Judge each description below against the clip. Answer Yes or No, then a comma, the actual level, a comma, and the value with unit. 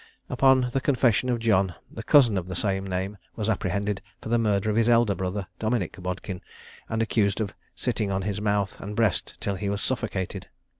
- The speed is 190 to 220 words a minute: Yes, average, 195 wpm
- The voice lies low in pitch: Yes, low, 105 Hz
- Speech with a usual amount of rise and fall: Yes, average, 3.0 semitones